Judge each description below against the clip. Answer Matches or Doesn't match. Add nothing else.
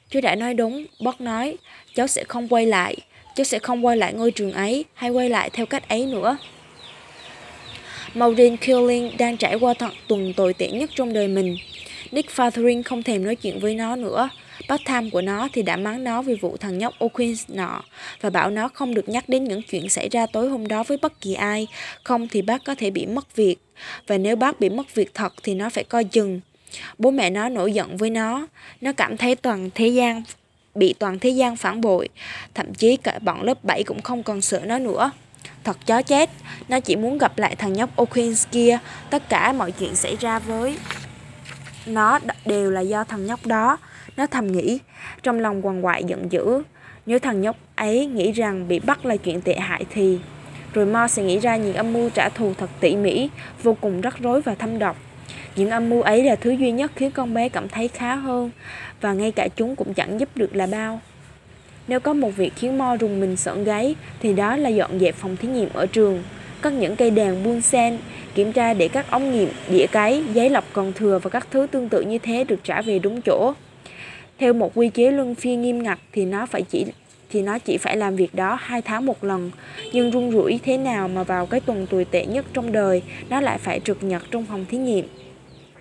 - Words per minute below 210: Doesn't match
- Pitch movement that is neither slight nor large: Matches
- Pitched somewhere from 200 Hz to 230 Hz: Matches